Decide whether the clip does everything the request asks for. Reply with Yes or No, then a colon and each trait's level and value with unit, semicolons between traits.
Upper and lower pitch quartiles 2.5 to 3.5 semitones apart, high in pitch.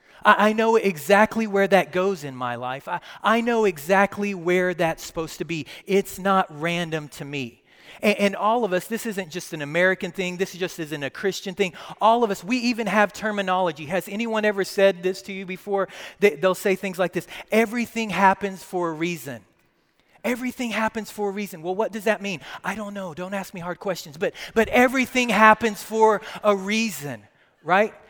Yes: average, 3.0 semitones; high, 195 Hz